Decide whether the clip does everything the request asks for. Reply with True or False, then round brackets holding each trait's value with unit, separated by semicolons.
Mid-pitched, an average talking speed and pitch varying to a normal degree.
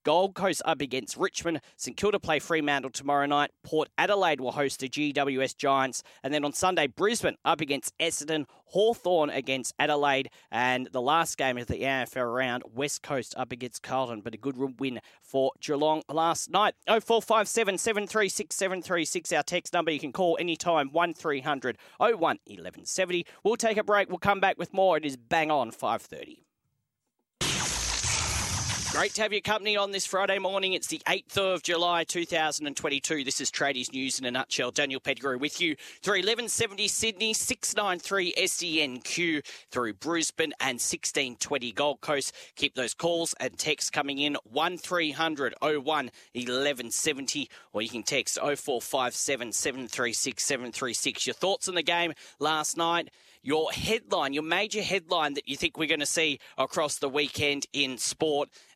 True (155 Hz; 170 wpm; 4.7 semitones)